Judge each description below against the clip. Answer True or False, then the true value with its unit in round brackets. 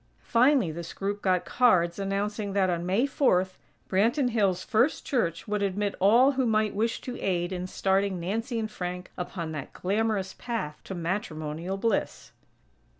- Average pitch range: True (3.8 semitones)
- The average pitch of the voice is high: True (195 Hz)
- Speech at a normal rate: True (155 wpm)